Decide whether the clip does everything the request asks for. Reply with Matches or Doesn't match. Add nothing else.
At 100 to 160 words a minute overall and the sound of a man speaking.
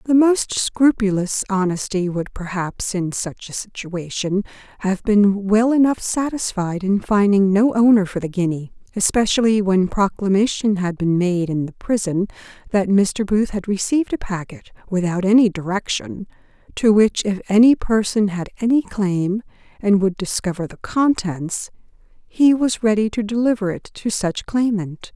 Doesn't match